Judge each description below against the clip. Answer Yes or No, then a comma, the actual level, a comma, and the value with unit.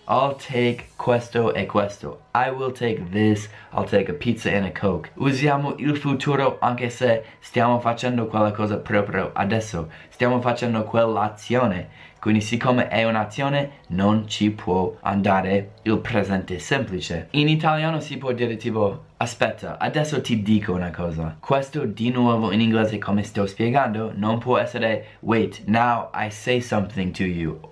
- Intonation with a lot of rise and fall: No, average, 3.1 semitones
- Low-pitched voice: Yes, low, 110 Hz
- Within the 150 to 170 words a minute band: Yes, average, 155 wpm